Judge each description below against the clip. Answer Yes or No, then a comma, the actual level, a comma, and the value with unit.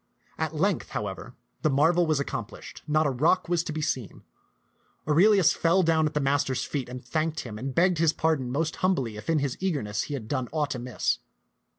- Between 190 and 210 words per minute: Yes, average, 200 wpm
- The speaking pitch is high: No, medium, 150 Hz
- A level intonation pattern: No, average, 4.0 semitones